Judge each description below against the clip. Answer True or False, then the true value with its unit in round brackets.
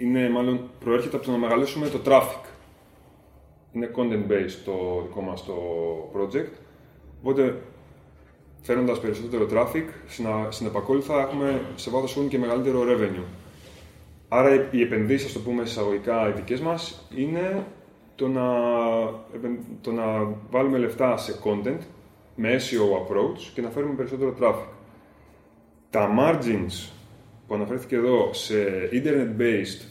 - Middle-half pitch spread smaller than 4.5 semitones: True (4.1 semitones)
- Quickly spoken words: False (130 wpm)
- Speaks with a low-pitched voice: True (120 Hz)